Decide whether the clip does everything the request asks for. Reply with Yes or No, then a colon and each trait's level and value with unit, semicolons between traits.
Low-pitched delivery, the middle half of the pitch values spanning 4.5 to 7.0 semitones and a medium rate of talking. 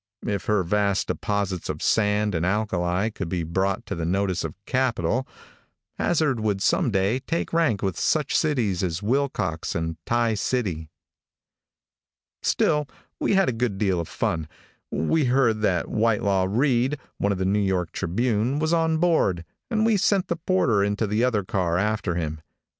Yes: low, 105 Hz; wide, 5.6 semitones; average, 160 wpm